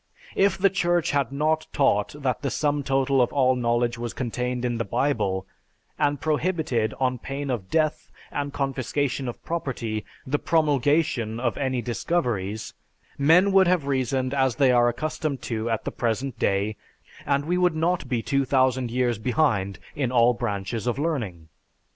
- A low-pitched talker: Yes, low, 130 Hz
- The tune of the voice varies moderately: Yes, average, 3.8 semitones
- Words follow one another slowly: No, average, 160 wpm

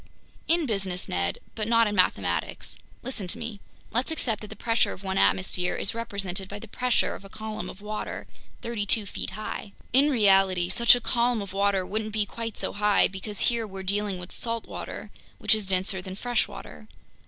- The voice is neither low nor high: No, high, 205 Hz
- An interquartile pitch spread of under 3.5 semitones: Yes, average, 3.1 semitones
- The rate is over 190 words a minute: Yes, average, 200 wpm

